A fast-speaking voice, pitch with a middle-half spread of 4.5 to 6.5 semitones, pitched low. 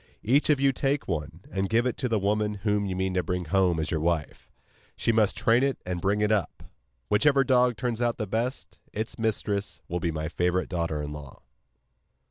Yes: fast, 210 wpm; average, 5.1 semitones; low, 105 Hz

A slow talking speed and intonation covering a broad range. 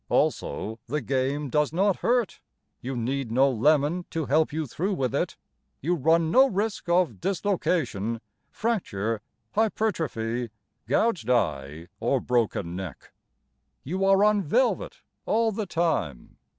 Yes: slow, 130 wpm; wide, 8.6 semitones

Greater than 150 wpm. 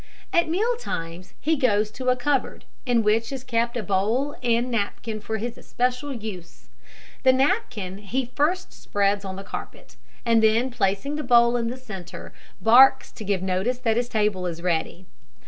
Yes: average, 175 wpm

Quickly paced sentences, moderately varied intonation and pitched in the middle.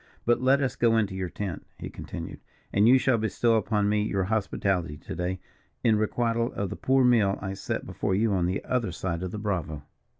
No: fast, 220 wpm; average, 3.6 semitones; low, 105 Hz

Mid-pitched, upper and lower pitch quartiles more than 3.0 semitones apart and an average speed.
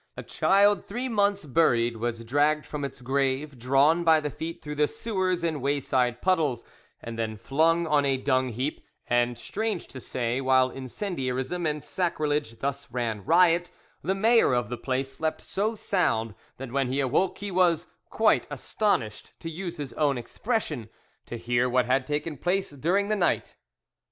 Yes: medium, 145 Hz; wide, 5.5 semitones; average, 170 wpm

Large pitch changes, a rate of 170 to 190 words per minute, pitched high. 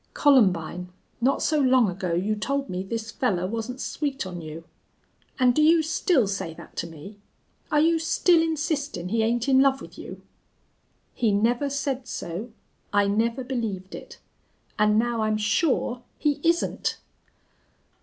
No: wide, 5.8 semitones; average, 155 wpm; high, 235 Hz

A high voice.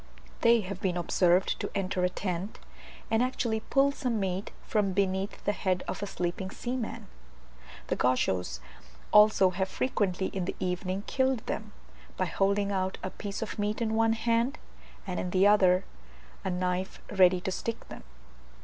Yes: high, 195 Hz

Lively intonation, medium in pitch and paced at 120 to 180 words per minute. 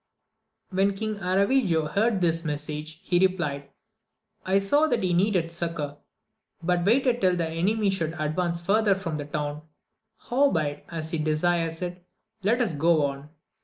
No: average, 4.1 semitones; medium, 175 Hz; average, 150 wpm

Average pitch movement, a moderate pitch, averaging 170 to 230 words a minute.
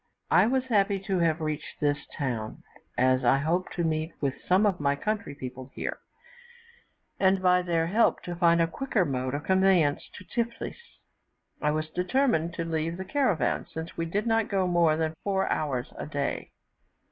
Yes: average, 4.3 semitones; medium, 170 Hz; average, 180 wpm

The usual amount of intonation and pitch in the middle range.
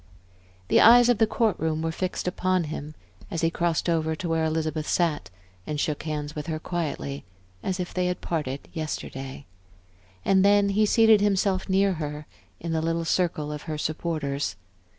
Yes: average, 3.4 semitones; medium, 165 Hz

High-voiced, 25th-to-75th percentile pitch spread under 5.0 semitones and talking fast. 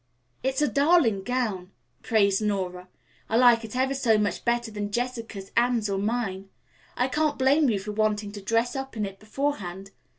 No: high, 225 Hz; average, 4.0 semitones; average, 175 wpm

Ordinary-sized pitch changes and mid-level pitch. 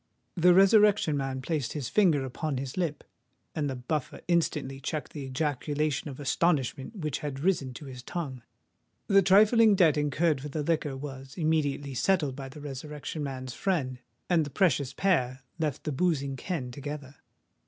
Yes: average, 3.9 semitones; medium, 145 Hz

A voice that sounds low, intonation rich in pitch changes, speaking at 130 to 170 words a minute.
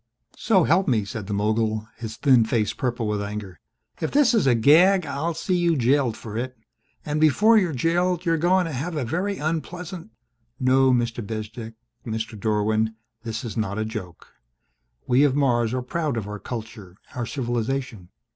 No: low, 125 Hz; wide, 6.2 semitones; average, 180 wpm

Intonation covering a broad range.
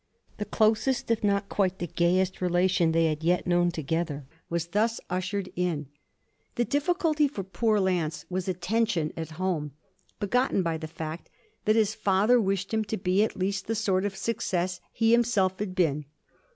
No: average, 3.9 semitones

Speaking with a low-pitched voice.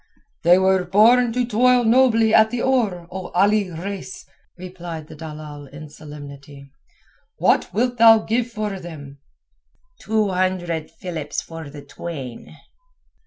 No: medium, 185 Hz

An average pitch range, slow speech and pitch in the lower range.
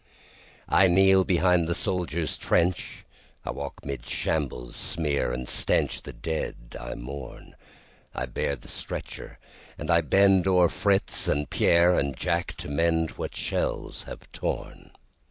Yes: average, 4.2 semitones; slow, 120 wpm; very low, 80 Hz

